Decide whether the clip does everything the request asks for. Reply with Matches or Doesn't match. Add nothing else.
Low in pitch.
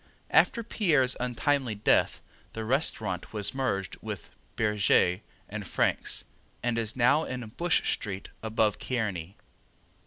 Matches